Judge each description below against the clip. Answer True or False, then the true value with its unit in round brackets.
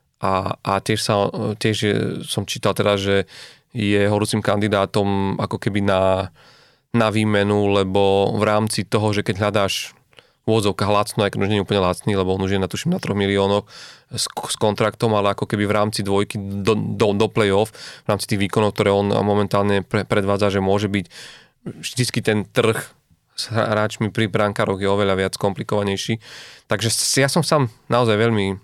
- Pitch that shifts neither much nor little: False (1.6 semitones)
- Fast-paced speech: True (170 wpm)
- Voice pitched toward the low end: True (105 Hz)